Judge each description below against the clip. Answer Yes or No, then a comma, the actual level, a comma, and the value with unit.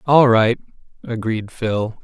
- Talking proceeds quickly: No, slow, 120 wpm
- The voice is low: Yes, low, 115 Hz